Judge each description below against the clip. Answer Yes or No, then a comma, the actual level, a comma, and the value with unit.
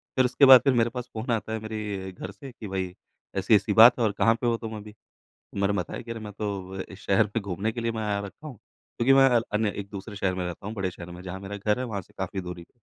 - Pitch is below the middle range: Yes, low, 105 Hz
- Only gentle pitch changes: No, average, 3.2 semitones